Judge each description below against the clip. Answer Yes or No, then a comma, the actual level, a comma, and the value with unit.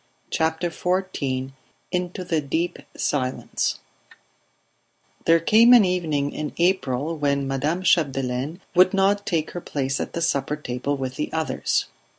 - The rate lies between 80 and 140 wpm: Yes, slow, 135 wpm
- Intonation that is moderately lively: Yes, average, 4.5 semitones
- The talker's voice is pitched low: No, medium, 160 Hz